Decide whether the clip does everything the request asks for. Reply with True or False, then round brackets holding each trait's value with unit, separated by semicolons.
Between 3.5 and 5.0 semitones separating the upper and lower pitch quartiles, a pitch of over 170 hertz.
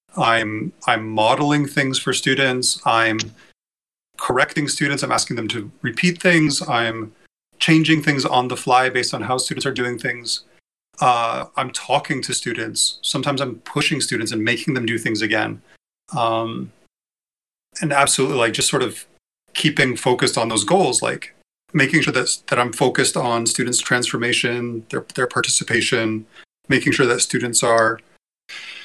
False (3.8 semitones; 125 Hz)